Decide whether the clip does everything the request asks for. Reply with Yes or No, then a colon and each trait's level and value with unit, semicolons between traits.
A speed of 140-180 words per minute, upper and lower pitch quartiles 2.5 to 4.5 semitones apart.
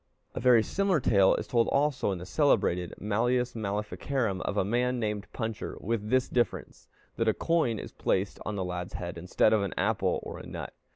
No: average, 195 wpm; average, 4.0 semitones